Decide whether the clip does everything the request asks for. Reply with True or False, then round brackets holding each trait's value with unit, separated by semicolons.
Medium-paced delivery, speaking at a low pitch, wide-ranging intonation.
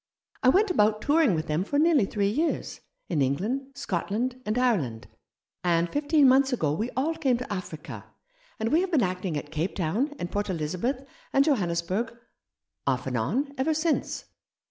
False (180 wpm; 220 Hz; 8.2 semitones)